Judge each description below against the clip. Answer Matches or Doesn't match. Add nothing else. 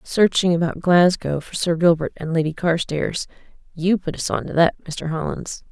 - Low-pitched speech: Doesn't match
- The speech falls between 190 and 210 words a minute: Doesn't match